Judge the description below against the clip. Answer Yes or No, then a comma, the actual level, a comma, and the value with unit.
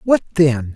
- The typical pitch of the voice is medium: Yes, medium, 155 Hz